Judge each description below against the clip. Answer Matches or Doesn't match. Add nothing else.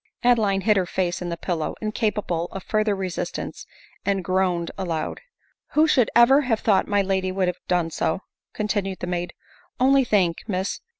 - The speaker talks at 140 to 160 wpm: Doesn't match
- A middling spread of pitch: Matches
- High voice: Matches